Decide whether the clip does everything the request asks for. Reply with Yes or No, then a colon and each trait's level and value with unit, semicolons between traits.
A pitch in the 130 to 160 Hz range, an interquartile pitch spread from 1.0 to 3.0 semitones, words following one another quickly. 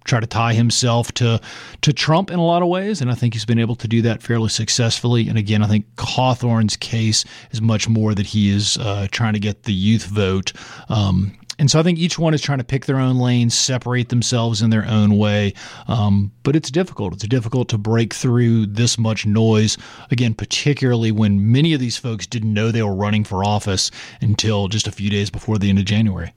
No: low, 115 Hz; average, 2.7 semitones; fast, 225 wpm